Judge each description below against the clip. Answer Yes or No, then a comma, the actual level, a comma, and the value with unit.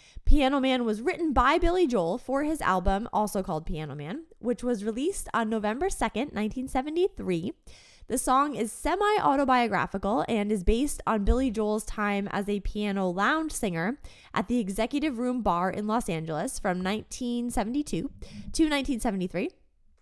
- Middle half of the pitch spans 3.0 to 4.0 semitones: No, average, 5.1 semitones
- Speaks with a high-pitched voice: Yes, high, 230 Hz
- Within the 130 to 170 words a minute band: Yes, average, 150 wpm